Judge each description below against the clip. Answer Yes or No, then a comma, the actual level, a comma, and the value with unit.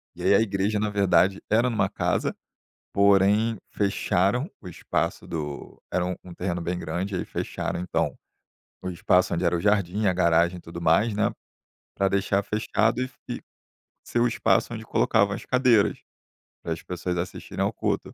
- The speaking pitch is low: Yes, low, 100 Hz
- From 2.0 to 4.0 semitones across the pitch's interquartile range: Yes, average, 3.3 semitones